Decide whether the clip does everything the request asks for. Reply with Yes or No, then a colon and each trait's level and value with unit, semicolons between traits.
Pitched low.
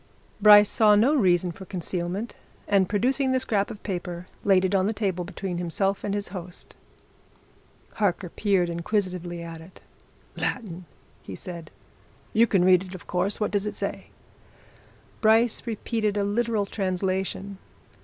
No: high, 195 Hz